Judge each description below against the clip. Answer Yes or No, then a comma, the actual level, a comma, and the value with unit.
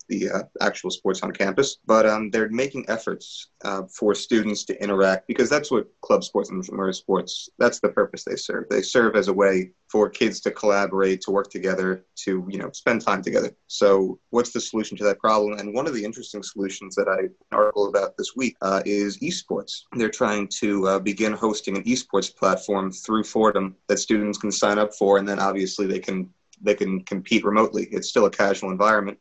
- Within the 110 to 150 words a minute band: No, fast, 205 wpm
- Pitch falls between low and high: No, low, 100 Hz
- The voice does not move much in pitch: Yes, narrow, 2.0 semitones